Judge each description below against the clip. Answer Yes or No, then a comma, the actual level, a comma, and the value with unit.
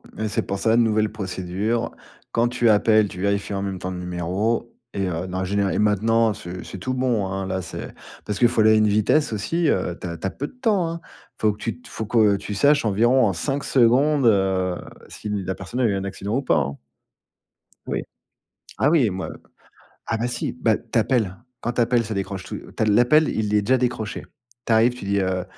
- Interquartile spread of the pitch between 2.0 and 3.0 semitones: No, average, 3.7 semitones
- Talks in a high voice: No, low, 110 Hz